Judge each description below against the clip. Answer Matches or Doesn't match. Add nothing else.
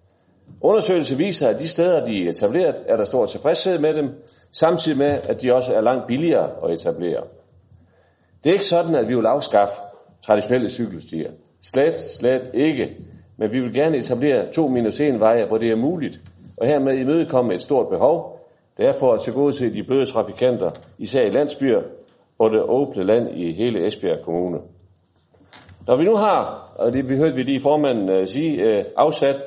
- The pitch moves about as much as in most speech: Doesn't match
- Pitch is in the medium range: Doesn't match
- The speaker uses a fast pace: Doesn't match